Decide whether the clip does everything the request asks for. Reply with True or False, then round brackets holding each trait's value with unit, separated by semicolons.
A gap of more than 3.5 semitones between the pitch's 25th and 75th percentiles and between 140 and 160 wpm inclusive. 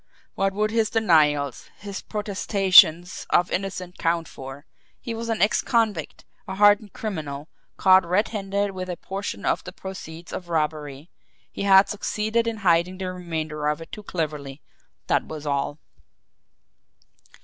True (4.5 semitones; 150 wpm)